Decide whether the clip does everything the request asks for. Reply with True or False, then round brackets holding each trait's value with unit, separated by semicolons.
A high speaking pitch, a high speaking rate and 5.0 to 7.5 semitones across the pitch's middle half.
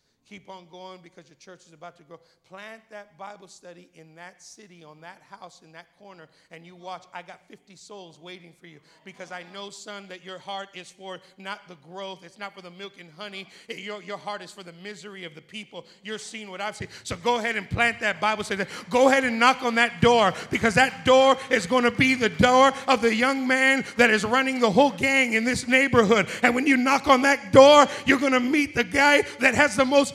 True (205 Hz; 240 wpm; 5.5 semitones)